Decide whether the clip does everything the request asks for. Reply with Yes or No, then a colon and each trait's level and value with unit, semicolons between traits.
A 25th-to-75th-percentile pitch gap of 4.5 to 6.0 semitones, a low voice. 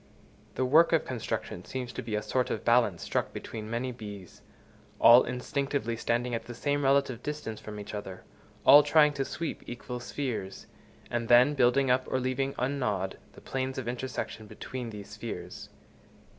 No: average, 3.2 semitones; low, 125 Hz